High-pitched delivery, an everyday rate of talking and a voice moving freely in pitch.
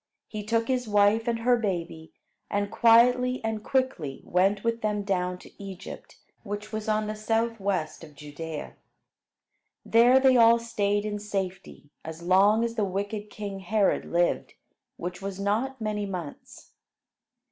No: high, 205 Hz; average, 145 wpm; average, 3.2 semitones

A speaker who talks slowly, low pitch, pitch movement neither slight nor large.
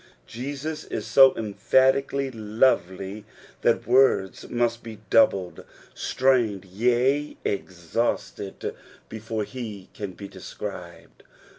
Yes: slow, 95 wpm; low, 115 Hz; average, 4.7 semitones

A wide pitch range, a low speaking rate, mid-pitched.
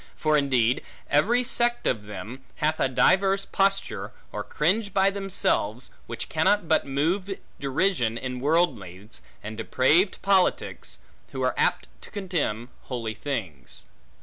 Yes: wide, 8.7 semitones; slow, 130 wpm; medium, 150 Hz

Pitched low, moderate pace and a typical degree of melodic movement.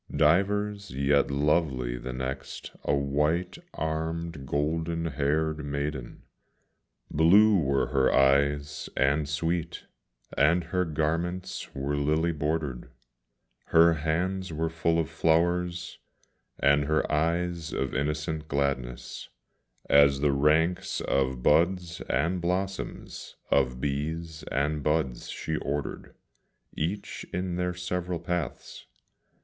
No: very low, 80 Hz; slow, 110 wpm; average, 3.2 semitones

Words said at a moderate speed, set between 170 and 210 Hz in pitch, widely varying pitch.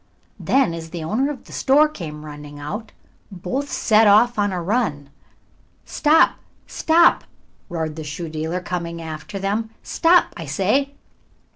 Yes: average, 150 wpm; medium, 185 Hz; wide, 7.4 semitones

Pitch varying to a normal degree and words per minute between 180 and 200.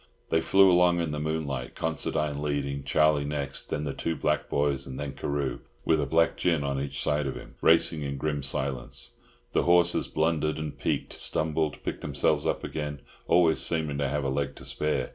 No: narrow, 2.2 semitones; average, 195 wpm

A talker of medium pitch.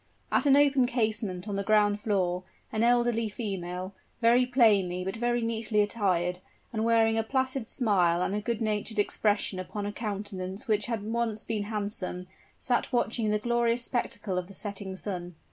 No: high, 215 Hz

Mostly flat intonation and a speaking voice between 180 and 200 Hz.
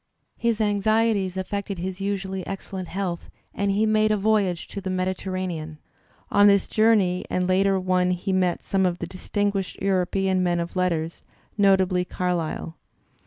Yes: narrow, 1.8 semitones; high, 190 Hz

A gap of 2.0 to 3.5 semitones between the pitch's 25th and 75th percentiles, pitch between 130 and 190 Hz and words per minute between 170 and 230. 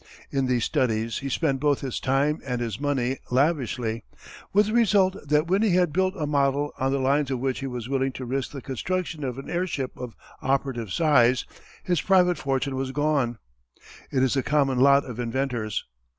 Yes: average, 3.0 semitones; low, 135 Hz; average, 195 wpm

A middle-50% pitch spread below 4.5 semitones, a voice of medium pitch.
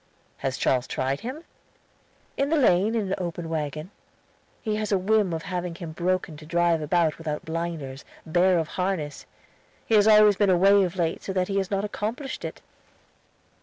Yes: average, 3.7 semitones; medium, 180 Hz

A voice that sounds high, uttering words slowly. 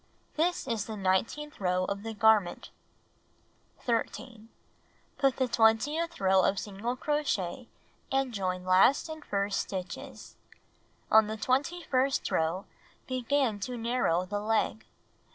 Yes: high, 225 Hz; slow, 125 wpm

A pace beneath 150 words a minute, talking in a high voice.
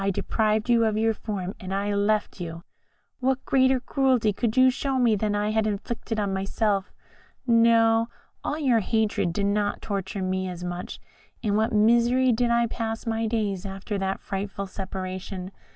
No: average, 170 wpm; high, 215 Hz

